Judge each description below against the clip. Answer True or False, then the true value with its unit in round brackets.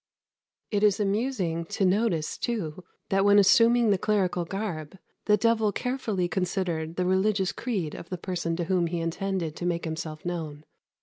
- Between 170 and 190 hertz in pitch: True (185 Hz)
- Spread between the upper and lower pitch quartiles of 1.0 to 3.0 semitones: False (3.7 semitones)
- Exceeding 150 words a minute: True (170 wpm)